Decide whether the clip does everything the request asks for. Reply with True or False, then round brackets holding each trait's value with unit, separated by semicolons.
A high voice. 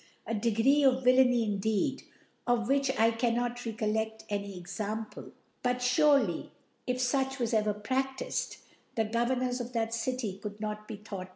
True (230 Hz)